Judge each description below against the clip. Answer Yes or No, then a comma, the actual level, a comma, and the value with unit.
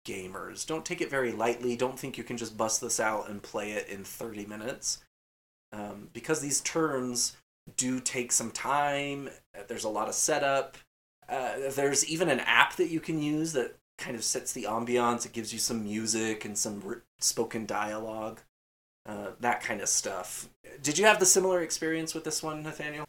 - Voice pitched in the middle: No, low, 125 Hz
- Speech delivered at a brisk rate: No, average, 190 wpm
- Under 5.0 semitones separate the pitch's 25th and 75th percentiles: No, wide, 5.6 semitones